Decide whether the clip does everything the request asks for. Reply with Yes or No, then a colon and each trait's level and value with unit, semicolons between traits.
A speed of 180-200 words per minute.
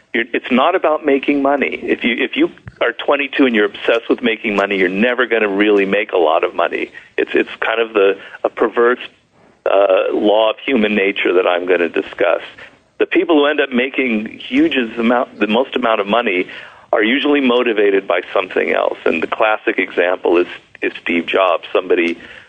Yes: average, 190 wpm